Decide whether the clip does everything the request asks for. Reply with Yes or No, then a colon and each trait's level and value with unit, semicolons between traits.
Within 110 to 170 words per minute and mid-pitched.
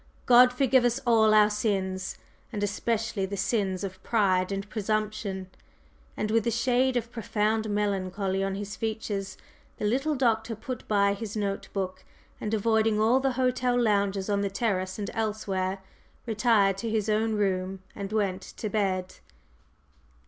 No: average, 155 wpm; high, 210 Hz